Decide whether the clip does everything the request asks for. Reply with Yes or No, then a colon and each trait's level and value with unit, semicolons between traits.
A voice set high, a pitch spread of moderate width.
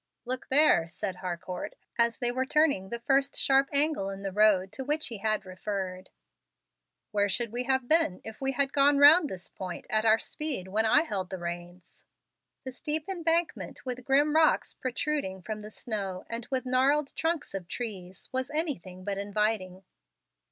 No: high, 235 Hz; wide, 6.4 semitones